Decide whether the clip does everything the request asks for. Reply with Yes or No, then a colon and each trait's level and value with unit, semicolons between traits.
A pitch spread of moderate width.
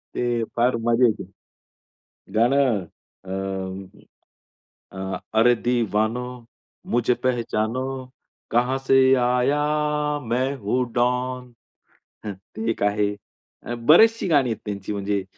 Yes: average, 3.5 semitones